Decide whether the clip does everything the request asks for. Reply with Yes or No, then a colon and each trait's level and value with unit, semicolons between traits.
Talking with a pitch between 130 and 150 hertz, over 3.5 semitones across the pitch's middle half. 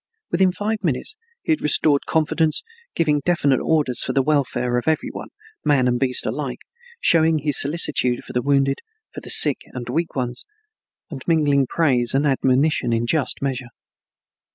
Yes: medium, 140 Hz; average, 3.9 semitones